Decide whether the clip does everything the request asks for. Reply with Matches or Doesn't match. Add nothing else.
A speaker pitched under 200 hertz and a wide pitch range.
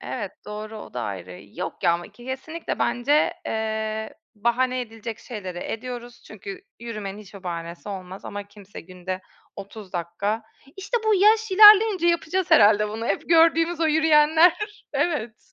Doesn't match